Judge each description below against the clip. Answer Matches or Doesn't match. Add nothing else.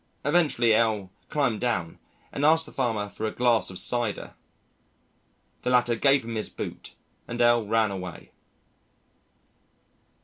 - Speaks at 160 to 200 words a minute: Doesn't match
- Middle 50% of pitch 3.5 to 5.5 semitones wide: Doesn't match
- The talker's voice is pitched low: Matches